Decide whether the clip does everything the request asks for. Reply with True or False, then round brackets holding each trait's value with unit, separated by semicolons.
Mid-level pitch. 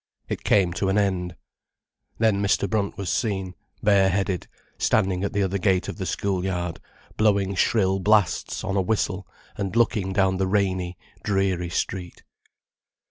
False (95 Hz)